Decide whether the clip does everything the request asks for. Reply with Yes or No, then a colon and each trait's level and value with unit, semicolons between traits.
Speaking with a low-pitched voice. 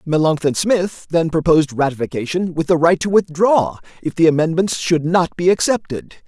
No: medium, 165 Hz